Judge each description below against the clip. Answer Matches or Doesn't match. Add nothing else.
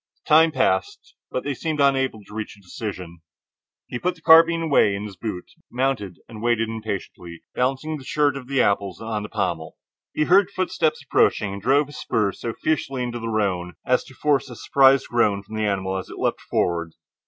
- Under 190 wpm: Doesn't match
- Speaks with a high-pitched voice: Doesn't match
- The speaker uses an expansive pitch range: Matches